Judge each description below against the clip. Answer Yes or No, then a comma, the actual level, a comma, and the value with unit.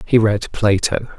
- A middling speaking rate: Yes, average, 150 wpm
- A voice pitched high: No, low, 105 Hz